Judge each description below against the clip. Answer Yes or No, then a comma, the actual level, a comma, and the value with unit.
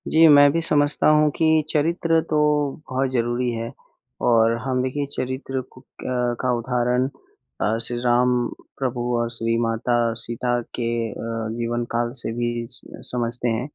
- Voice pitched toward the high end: No, low, 125 Hz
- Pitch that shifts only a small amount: Yes, narrow, 2.2 semitones